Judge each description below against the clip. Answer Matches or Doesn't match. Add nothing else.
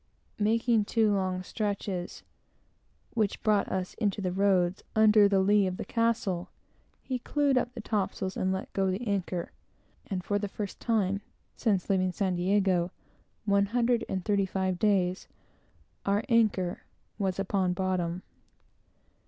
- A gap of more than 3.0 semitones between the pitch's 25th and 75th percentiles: Doesn't match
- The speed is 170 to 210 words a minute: Doesn't match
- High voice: Matches